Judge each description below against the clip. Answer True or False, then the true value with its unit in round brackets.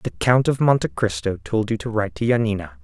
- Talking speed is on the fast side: True (235 wpm)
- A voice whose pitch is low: True (105 Hz)